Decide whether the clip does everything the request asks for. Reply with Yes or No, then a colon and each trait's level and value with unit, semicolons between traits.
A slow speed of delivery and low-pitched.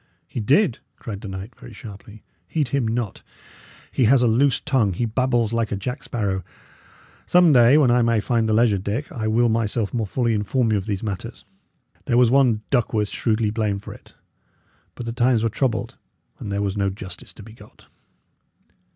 No: average, 195 wpm; low, 115 Hz